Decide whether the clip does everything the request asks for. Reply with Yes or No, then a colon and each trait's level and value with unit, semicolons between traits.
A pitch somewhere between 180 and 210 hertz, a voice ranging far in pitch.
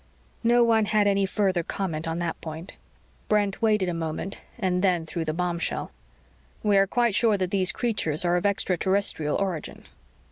No: high, 190 Hz; average, 3.2 semitones